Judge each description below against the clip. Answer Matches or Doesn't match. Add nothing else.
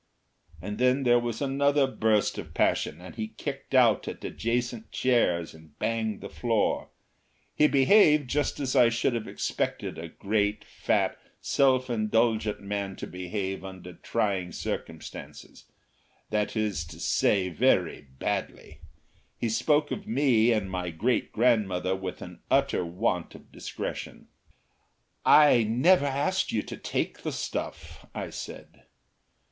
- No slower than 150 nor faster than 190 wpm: Doesn't match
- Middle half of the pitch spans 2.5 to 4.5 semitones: Doesn't match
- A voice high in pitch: Doesn't match